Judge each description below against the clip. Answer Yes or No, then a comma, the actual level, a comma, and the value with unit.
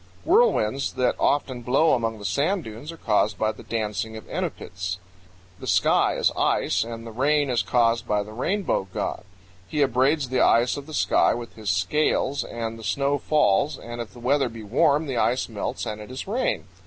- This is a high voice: No, low, 120 Hz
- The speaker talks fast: No, average, 195 wpm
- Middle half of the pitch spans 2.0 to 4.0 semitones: No, average, 4.5 semitones